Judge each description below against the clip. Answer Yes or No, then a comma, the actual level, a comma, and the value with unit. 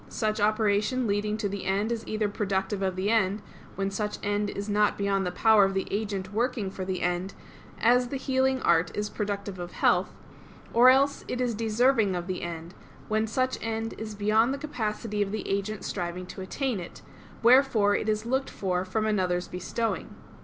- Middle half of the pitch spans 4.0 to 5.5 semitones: No, average, 2.7 semitones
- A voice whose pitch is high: Yes, high, 210 Hz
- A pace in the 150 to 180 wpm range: No, average, 190 wpm